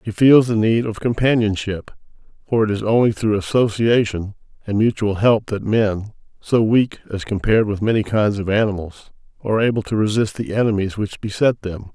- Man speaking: Yes, male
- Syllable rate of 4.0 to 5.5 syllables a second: Yes, 5.4 syllables/s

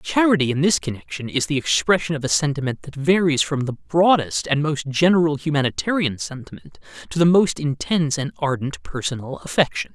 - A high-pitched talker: No, medium, 150 Hz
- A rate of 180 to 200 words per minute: No, average, 170 wpm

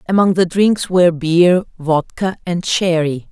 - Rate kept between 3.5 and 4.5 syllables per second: Yes, 4.1 syllables/s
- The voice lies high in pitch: No, medium, 175 Hz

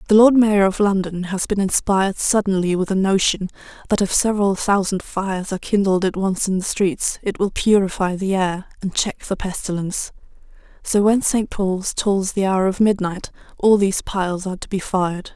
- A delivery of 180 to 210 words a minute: Yes, average, 190 wpm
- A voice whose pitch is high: Yes, high, 195 Hz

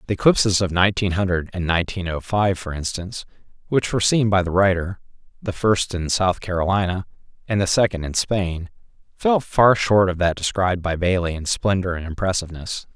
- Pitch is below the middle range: Yes, very low, 95 Hz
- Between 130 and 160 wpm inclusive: No, average, 180 wpm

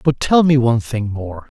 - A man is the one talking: Yes, male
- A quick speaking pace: Yes, fast, 225 wpm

